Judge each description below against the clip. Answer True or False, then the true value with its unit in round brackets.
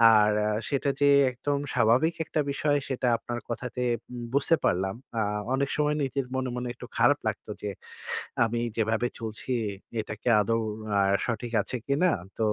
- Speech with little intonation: False (3.6 semitones)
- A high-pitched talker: False (125 Hz)